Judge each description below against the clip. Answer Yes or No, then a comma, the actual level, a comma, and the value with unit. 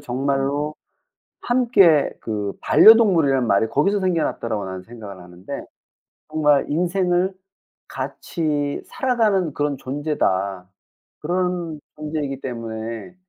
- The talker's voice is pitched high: No, medium, 145 Hz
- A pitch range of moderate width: No, wide, 7.4 semitones